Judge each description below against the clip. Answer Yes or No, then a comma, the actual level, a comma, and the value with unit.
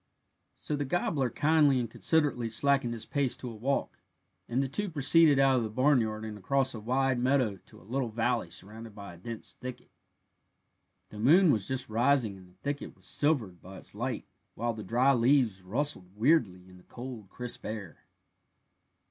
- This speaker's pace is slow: No, average, 180 wpm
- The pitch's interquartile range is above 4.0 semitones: Yes, average, 4.4 semitones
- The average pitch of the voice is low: Yes, low, 120 Hz